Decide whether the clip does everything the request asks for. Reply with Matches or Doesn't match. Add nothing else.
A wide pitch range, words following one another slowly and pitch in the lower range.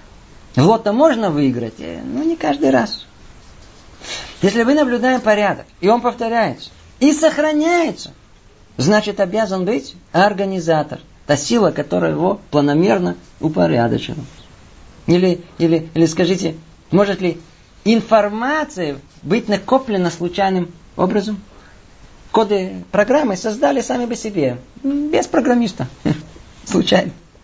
Doesn't match